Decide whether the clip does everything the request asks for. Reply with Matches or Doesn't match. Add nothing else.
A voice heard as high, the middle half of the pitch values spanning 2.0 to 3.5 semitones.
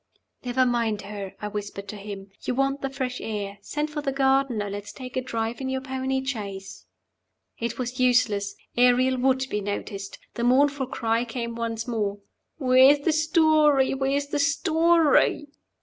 Doesn't match